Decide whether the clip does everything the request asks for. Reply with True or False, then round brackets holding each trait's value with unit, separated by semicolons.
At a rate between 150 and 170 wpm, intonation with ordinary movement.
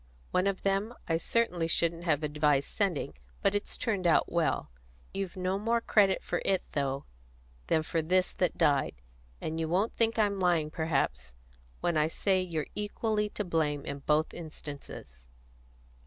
True (160 wpm; 4.3 semitones)